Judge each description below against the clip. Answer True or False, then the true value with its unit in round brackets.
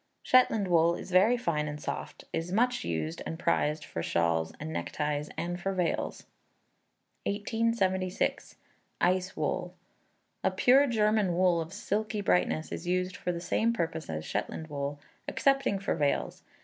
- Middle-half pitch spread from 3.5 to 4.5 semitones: False (5.2 semitones)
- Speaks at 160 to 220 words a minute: False (150 wpm)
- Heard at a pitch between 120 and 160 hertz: False (180 Hz)